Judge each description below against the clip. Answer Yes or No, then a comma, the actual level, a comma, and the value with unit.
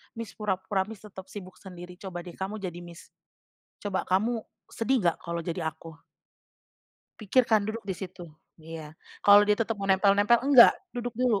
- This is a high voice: Yes, high, 195 Hz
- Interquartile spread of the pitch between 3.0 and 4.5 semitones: Yes, average, 3.4 semitones